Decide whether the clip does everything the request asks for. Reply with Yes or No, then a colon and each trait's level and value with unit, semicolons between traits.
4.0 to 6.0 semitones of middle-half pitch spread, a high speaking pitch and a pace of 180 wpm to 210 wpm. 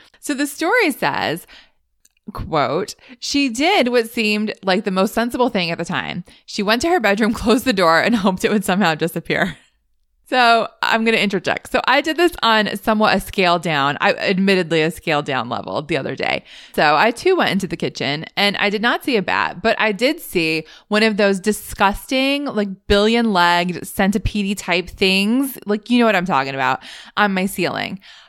Yes: average, 4.7 semitones; high, 210 Hz; average, 195 wpm